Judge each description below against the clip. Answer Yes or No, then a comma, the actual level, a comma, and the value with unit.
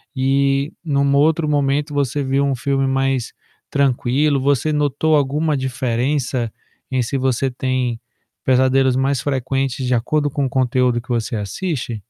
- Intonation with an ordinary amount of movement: No, narrow, 1.9 semitones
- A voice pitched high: No, low, 135 Hz